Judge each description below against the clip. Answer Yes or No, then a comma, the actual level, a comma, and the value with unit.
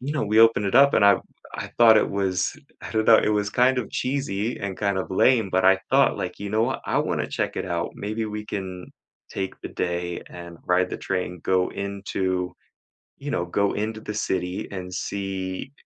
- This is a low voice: Yes, low, 100 Hz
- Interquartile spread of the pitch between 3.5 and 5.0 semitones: No, average, 2.9 semitones